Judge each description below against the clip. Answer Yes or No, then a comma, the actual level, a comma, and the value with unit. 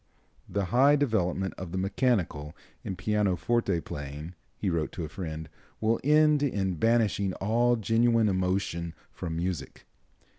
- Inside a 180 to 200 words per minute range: No, slow, 135 wpm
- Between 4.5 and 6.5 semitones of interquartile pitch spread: Yes, average, 5.2 semitones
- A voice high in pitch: No, very low, 95 Hz